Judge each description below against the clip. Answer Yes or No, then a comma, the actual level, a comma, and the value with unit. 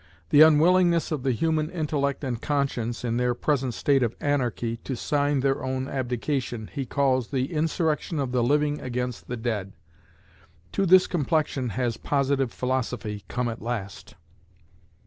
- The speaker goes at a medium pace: Yes, average, 150 wpm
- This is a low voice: Yes, low, 130 Hz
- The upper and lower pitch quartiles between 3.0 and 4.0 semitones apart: Yes, average, 3.4 semitones